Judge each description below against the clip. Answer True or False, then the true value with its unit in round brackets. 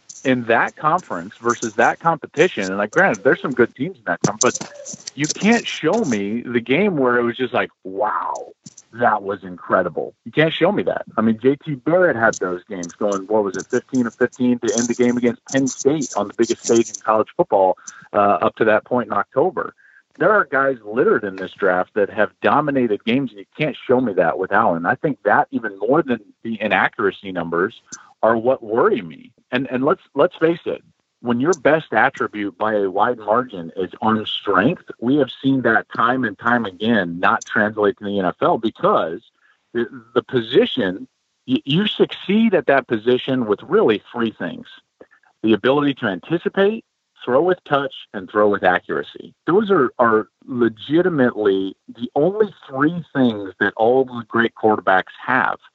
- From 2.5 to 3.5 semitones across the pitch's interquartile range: False (4.6 semitones)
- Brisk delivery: False (185 wpm)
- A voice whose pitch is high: False (120 Hz)